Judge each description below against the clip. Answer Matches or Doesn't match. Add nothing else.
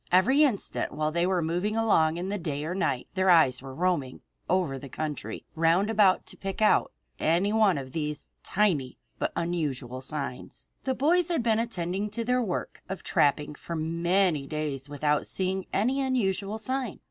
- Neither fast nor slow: Matches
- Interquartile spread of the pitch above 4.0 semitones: Matches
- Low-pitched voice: Doesn't match